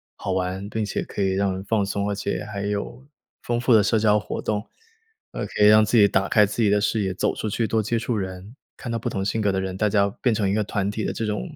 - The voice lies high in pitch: No, low, 105 Hz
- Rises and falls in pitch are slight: Yes, narrow, 1.8 semitones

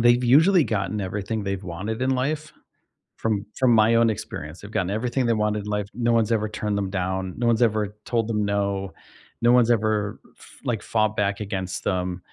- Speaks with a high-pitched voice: No, low, 105 Hz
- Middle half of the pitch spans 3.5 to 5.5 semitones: No, average, 2.9 semitones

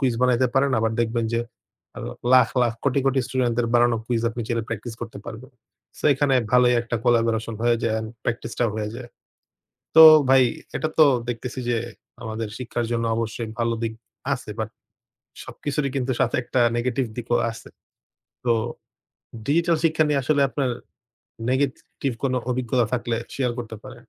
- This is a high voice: No, low, 120 Hz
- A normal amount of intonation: No, narrow, 2.1 semitones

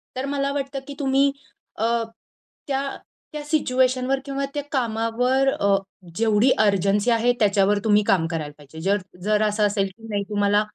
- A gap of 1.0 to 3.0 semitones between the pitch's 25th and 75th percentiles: No, average, 4.7 semitones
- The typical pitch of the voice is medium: No, high, 225 Hz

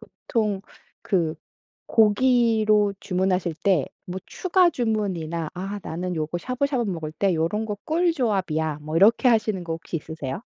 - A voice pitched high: Yes, high, 195 Hz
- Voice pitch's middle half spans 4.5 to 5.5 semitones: Yes, average, 5.1 semitones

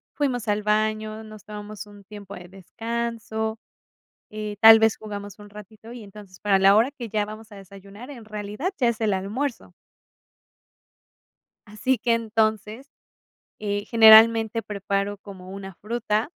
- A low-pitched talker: No, high, 215 Hz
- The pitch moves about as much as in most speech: No, narrow, 1.6 semitones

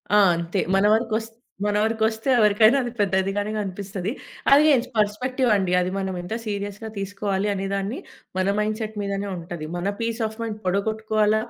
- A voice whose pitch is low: No, high, 210 Hz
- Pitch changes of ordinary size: No, narrow, 2.1 semitones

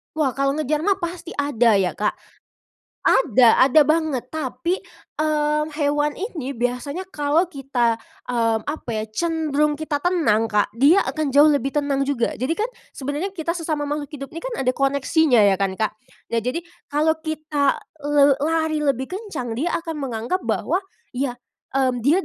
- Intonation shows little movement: No, average, 3.7 semitones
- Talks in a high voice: Yes, very high, 290 Hz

